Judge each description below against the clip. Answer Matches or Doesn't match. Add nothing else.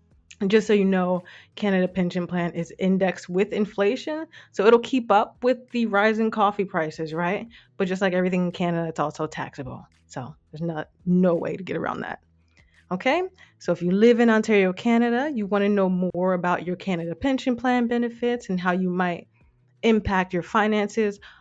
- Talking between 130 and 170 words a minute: Doesn't match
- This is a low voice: Doesn't match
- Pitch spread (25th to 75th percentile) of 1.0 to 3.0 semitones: Doesn't match